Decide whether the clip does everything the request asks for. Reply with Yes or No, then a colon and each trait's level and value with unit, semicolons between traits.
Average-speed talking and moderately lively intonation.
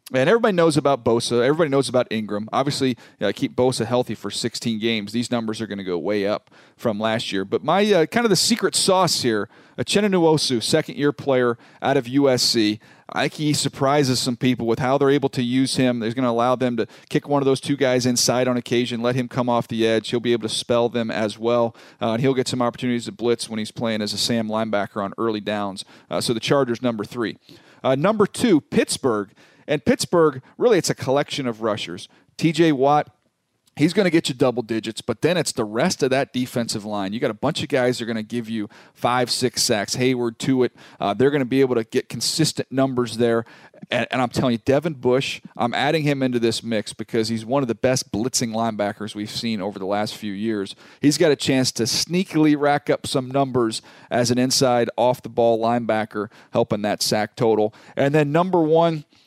No: fast, 220 wpm; average, 3.6 semitones